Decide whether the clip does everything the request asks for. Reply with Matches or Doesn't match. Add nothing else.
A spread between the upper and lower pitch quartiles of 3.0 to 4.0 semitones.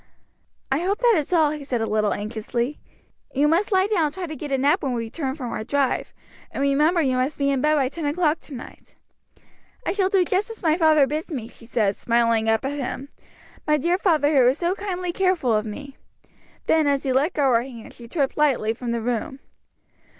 Doesn't match